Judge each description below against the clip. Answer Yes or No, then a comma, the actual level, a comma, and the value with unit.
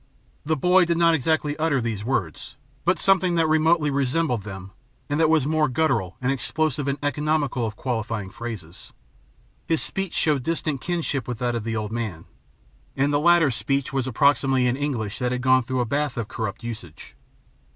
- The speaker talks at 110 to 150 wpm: No, average, 180 wpm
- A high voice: No, low, 135 Hz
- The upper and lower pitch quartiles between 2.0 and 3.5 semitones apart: No, average, 5.1 semitones